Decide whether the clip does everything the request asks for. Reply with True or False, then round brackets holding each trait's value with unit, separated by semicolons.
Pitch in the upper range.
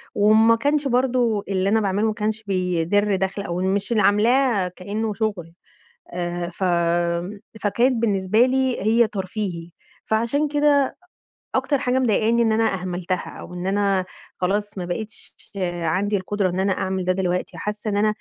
True (205 Hz)